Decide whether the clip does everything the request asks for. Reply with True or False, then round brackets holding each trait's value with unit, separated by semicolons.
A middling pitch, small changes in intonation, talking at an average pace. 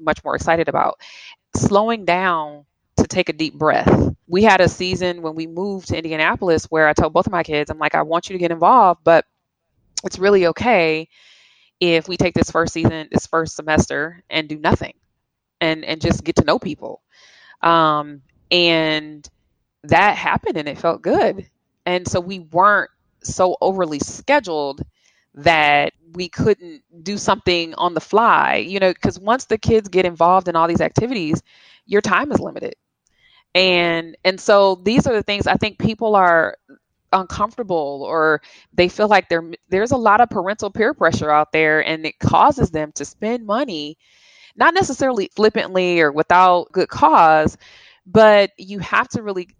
False (175 Hz; 4.1 semitones; 170 wpm)